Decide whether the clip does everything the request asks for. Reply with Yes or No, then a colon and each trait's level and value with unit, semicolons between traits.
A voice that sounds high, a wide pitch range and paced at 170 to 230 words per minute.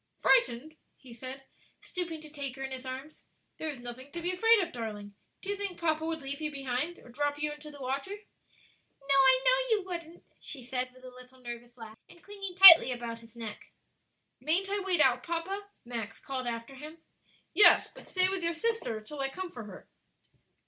Yes: very high, 290 Hz; wide, 5.7 semitones; fast, 205 wpm